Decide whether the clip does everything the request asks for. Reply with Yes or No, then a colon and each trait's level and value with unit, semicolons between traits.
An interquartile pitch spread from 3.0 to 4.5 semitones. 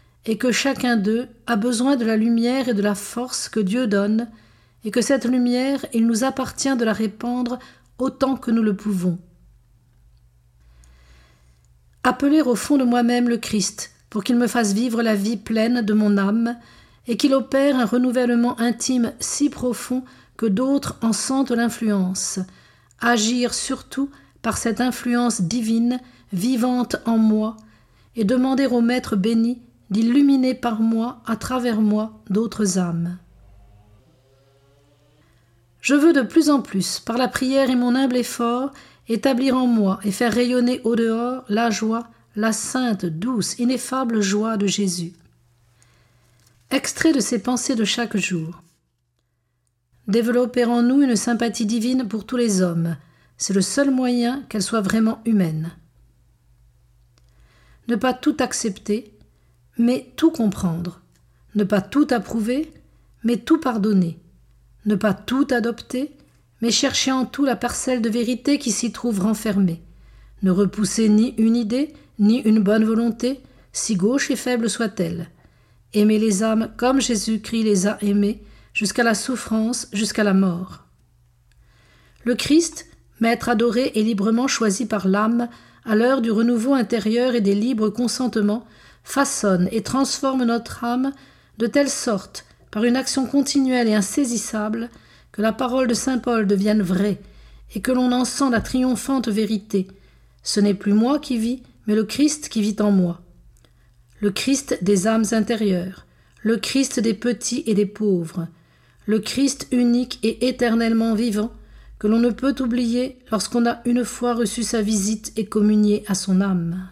Yes: average, 3.5 semitones